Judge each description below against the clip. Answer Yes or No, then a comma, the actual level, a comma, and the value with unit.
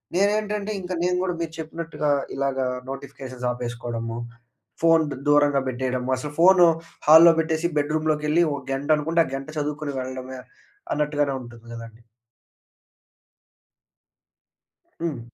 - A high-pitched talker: No, medium, 145 Hz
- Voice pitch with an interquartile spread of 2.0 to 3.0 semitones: No, average, 4.1 semitones